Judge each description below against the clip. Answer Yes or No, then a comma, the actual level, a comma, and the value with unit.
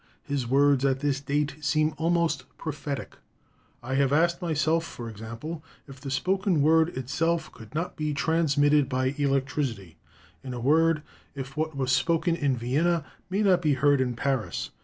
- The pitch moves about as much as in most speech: Yes, average, 3.5 semitones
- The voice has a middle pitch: Yes, medium, 145 Hz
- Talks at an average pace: Yes, average, 160 wpm